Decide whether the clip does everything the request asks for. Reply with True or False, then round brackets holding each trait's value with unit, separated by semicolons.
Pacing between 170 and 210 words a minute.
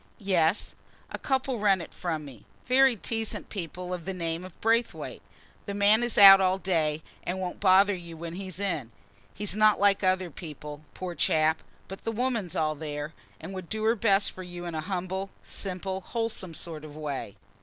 True (190 wpm)